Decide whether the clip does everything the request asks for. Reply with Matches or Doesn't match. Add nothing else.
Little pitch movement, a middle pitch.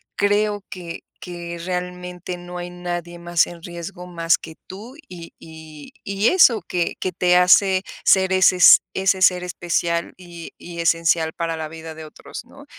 Matches